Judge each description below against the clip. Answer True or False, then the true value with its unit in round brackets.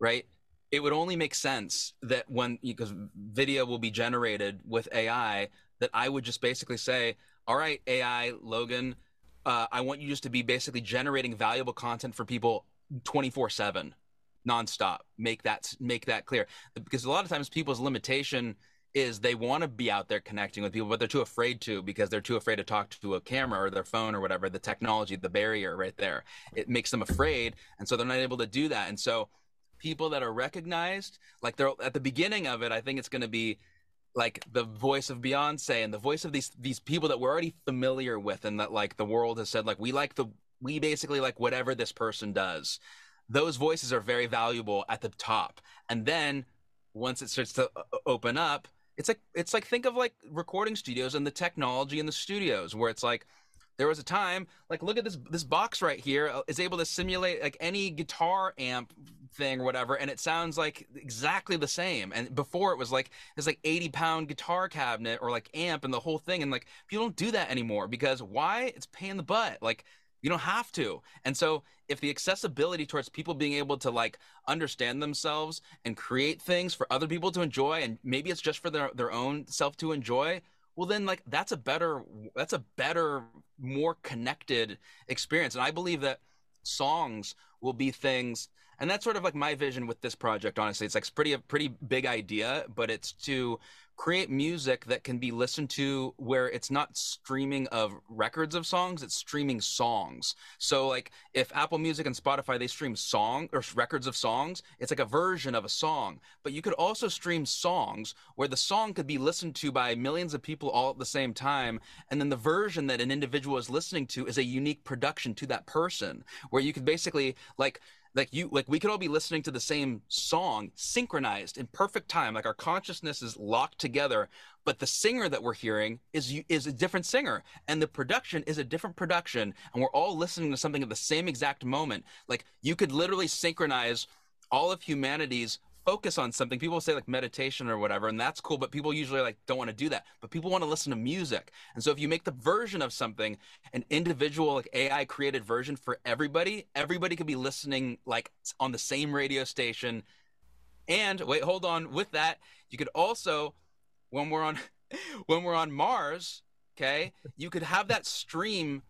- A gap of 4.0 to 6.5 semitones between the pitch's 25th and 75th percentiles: True (4.7 semitones)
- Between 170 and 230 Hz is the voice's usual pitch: False (140 Hz)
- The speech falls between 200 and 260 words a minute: True (205 wpm)